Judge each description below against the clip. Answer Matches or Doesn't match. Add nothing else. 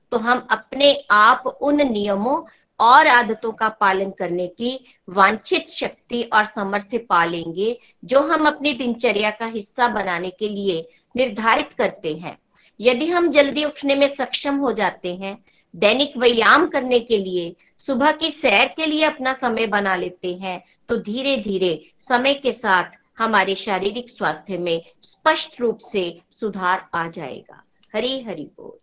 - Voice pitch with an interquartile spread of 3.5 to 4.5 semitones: Doesn't match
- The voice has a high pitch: Matches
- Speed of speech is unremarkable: Matches